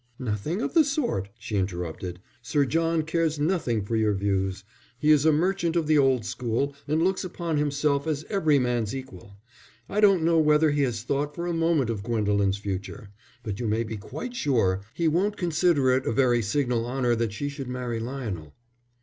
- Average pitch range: No, wide, 6.5 semitones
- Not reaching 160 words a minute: No, average, 190 wpm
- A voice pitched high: No, low, 135 Hz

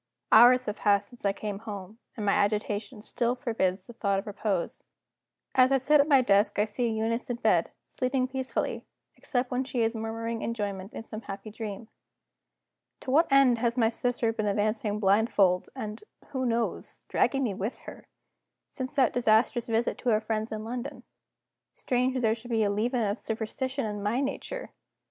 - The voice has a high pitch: Yes, high, 225 Hz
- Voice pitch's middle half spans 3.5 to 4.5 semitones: No, average, 3.1 semitones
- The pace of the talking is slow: No, average, 180 wpm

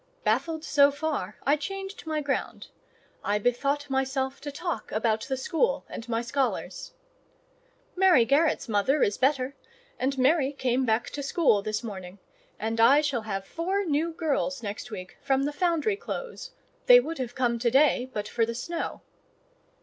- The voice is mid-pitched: No, very high, 270 Hz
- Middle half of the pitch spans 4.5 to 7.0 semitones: Yes, average, 5.2 semitones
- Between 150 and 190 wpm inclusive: Yes, average, 165 wpm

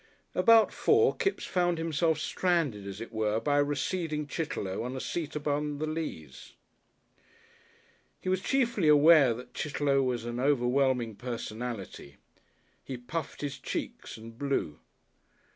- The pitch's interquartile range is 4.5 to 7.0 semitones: Yes, average, 5.2 semitones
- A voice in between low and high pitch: Yes, medium, 145 Hz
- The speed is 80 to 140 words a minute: Yes, slow, 135 wpm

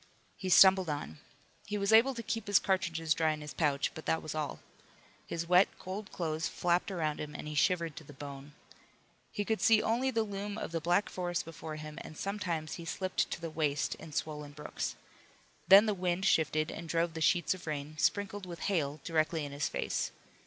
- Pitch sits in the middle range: Yes, medium, 165 Hz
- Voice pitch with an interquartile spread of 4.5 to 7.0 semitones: No, average, 3.9 semitones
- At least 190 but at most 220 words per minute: Yes, fast, 205 wpm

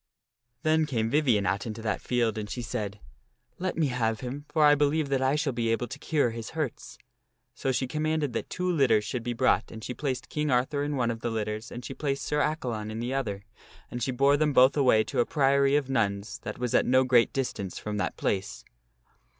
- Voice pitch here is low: Yes, low, 125 Hz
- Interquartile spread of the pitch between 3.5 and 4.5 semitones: Yes, average, 4.2 semitones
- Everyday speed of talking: No, fast, 230 wpm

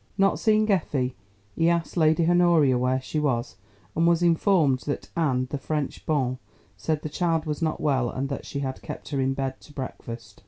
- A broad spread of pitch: No, average, 4.1 semitones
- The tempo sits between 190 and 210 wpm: Yes, average, 195 wpm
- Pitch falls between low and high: Yes, medium, 150 Hz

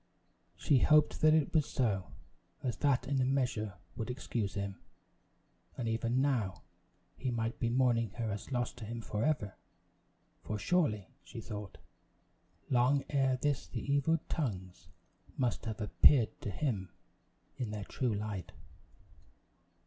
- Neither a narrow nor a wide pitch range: Yes, average, 4.2 semitones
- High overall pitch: No, low, 120 Hz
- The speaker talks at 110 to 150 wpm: Yes, average, 140 wpm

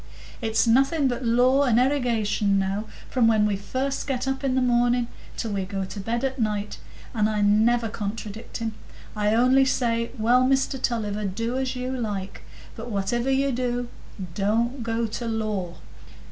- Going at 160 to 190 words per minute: Yes, average, 170 wpm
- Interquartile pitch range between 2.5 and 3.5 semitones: Yes, average, 3.2 semitones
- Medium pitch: No, high, 230 Hz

